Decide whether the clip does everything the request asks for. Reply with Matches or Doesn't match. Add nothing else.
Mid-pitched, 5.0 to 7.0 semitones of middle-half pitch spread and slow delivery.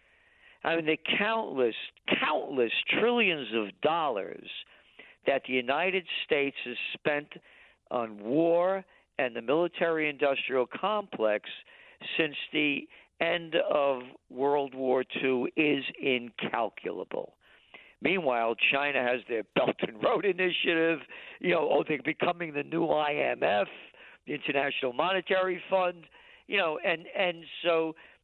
Matches